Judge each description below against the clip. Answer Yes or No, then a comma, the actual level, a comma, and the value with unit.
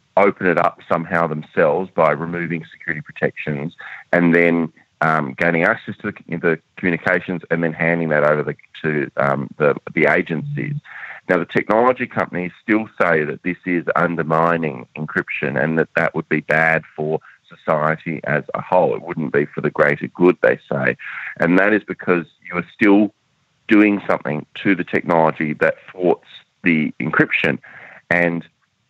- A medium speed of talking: Yes, average, 160 wpm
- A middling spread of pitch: No, narrow, 2.3 semitones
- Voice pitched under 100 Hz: Yes, very low, 85 Hz